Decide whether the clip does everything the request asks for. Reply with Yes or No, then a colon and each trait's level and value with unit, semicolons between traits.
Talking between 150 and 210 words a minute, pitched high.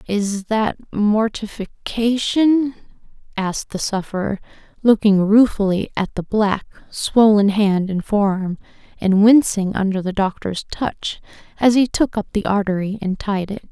No: slow, 135 wpm; high, 205 Hz